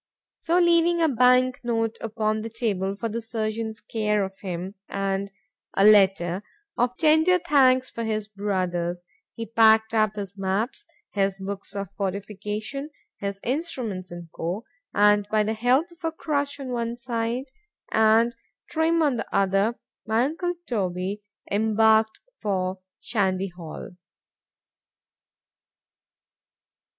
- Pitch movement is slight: No, average, 4.0 semitones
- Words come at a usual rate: No, slow, 120 wpm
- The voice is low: No, high, 220 Hz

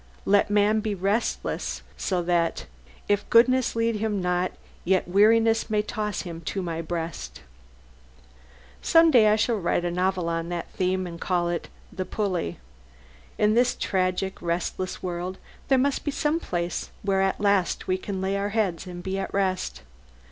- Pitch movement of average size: Yes, average, 3.2 semitones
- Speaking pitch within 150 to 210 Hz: Yes, high, 190 Hz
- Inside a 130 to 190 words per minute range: Yes, average, 165 wpm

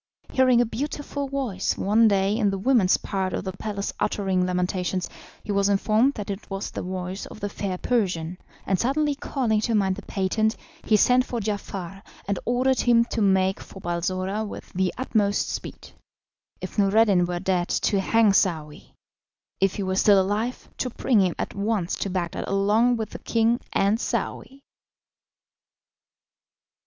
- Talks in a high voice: Yes, high, 200 Hz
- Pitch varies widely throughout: No, average, 3.3 semitones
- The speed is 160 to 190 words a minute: Yes, average, 165 wpm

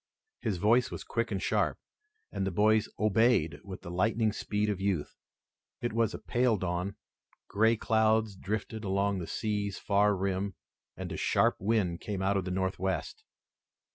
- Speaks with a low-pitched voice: Yes, low, 100 Hz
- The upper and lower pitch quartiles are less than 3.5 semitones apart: Yes, narrow, 2.5 semitones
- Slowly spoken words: No, average, 165 wpm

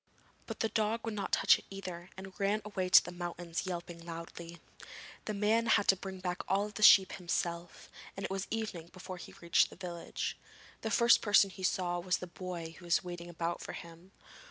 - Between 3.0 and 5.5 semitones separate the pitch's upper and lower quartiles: No, narrow, 2.4 semitones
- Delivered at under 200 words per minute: No, fast, 205 wpm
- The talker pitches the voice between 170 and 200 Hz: Yes, medium, 185 Hz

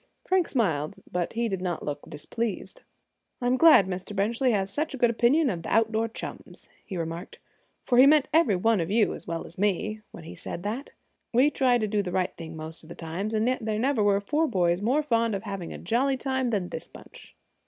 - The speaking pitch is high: Yes, high, 215 Hz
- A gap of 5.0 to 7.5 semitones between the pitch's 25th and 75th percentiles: Yes, wide, 5.4 semitones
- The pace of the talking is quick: Yes, fast, 215 wpm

